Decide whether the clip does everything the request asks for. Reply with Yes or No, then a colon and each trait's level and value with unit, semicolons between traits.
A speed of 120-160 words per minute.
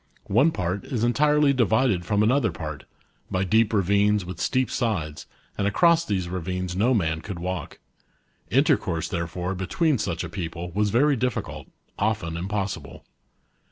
Yes: average, 145 wpm